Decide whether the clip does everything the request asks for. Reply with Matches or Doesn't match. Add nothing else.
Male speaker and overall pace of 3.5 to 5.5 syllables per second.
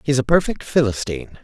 Doesn't match